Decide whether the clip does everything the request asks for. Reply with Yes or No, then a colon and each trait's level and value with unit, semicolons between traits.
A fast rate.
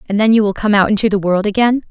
Yes: fast, 315 wpm